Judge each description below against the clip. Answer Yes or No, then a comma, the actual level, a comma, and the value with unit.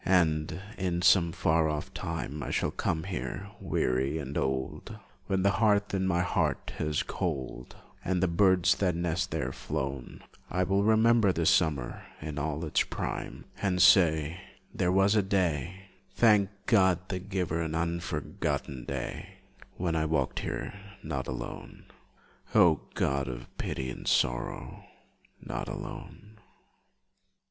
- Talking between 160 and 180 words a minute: No, average, 140 wpm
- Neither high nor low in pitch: No, very low, 85 Hz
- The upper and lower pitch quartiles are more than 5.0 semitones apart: No, average, 3.8 semitones